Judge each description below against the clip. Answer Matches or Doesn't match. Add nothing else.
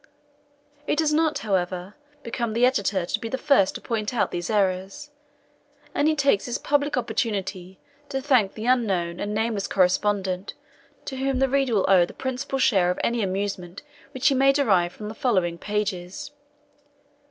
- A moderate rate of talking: Matches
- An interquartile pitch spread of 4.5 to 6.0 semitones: Matches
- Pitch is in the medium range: Doesn't match